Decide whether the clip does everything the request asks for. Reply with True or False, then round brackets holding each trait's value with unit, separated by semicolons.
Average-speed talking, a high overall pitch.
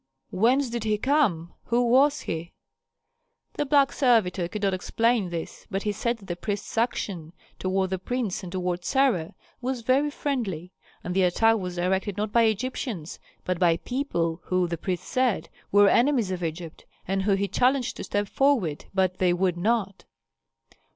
True (170 wpm; 200 Hz)